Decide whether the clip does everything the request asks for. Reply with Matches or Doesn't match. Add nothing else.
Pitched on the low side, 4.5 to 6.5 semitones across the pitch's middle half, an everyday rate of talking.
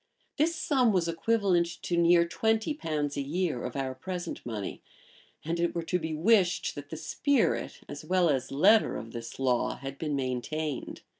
Doesn't match